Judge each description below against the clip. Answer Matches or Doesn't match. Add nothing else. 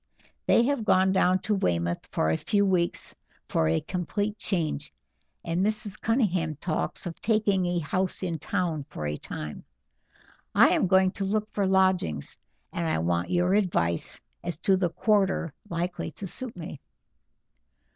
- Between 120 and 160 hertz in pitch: Doesn't match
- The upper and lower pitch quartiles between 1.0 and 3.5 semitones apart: Doesn't match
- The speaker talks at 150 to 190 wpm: Matches